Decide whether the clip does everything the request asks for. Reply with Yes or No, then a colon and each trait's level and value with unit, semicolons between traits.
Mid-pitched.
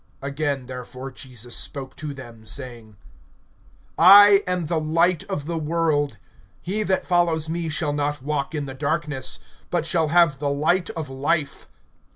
Yes: medium, 150 Hz